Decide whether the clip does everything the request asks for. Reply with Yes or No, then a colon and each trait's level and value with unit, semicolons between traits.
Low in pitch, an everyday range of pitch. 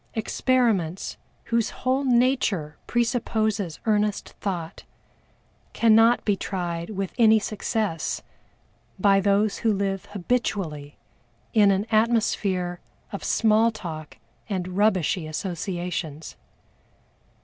No: high, 200 Hz; average, 3.8 semitones